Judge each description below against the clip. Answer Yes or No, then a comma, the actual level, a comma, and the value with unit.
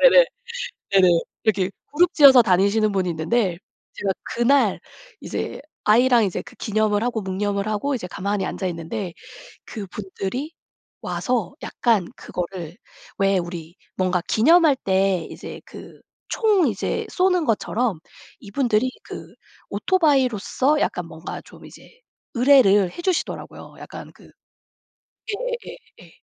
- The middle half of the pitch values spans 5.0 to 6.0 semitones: Yes, wide, 5.6 semitones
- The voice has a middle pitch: No, high, 210 Hz